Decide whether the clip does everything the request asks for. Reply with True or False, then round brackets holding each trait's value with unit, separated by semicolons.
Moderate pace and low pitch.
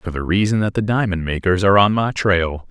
False (245 wpm; 95 Hz)